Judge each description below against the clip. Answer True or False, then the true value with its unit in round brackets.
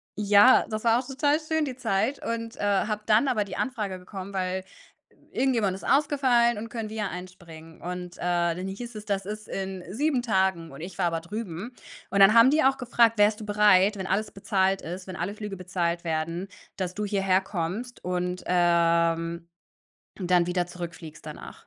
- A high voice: True (195 Hz)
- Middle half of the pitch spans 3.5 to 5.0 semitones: True (4.1 semitones)